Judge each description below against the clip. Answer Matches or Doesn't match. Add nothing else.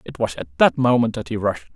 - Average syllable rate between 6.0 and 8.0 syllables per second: Matches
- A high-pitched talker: Doesn't match